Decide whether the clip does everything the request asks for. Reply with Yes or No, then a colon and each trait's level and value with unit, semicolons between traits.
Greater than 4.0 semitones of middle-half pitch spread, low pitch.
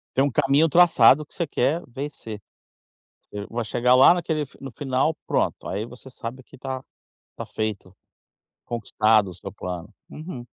Yes: average, 4.9 semitones; low, 130 Hz